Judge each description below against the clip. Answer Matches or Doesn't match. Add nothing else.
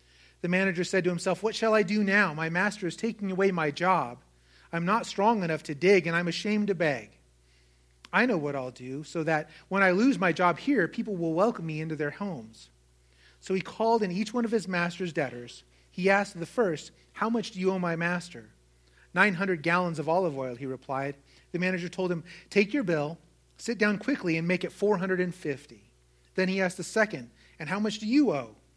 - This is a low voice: Doesn't match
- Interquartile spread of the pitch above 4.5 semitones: Matches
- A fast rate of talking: Matches